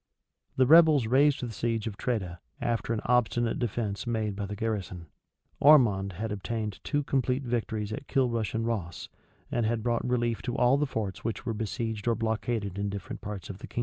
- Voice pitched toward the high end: No, low, 115 Hz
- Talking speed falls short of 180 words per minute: No, average, 190 wpm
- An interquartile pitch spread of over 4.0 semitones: No, average, 2.8 semitones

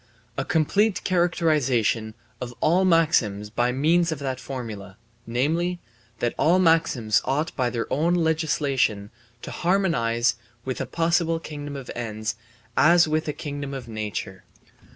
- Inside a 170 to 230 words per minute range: No, slow, 135 wpm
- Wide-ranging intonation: Yes, wide, 5.8 semitones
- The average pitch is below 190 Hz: Yes, medium, 140 Hz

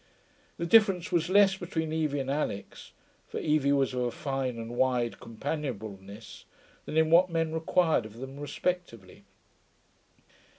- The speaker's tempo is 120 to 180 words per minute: Yes, average, 140 wpm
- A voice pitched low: No, medium, 145 Hz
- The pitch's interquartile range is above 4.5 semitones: Yes, wide, 5.5 semitones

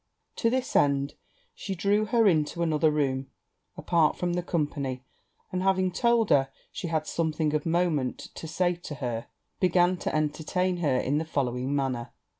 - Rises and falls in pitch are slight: No, average, 4.3 semitones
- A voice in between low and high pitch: Yes, medium, 160 Hz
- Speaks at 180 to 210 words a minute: No, average, 165 wpm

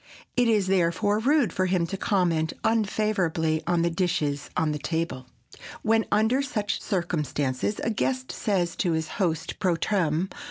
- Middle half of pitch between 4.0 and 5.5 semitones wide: Yes, average, 4.6 semitones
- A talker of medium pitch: Yes, medium, 180 Hz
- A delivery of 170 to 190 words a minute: No, average, 155 wpm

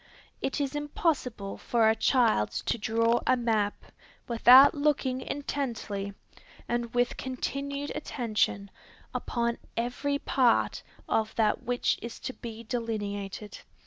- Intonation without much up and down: No, average, 3.2 semitones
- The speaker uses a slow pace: Yes, slow, 115 wpm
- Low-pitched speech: No, high, 235 Hz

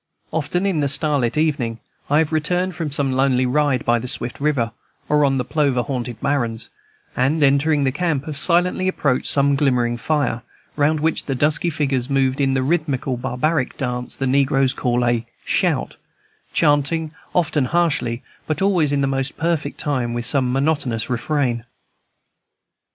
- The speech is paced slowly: No, average, 160 wpm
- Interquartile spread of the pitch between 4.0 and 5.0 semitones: No, average, 3.4 semitones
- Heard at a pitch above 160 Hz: No, medium, 140 Hz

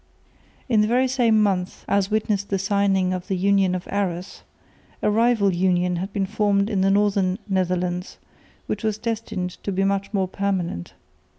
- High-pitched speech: Yes, high, 195 Hz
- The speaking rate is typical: Yes, average, 170 wpm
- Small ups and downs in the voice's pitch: Yes, narrow, 2.3 semitones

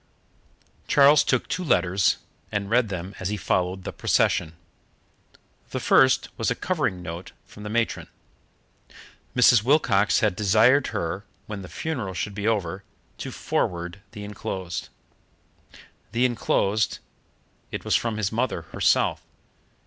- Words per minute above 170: No, slow, 135 wpm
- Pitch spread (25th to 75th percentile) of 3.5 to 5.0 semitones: Yes, average, 4.2 semitones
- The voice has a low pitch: Yes, low, 105 Hz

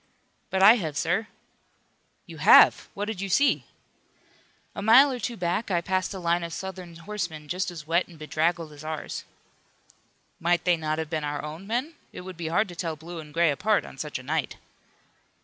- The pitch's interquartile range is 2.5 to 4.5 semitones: Yes, average, 3.4 semitones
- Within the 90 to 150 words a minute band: No, average, 200 wpm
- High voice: No, medium, 175 Hz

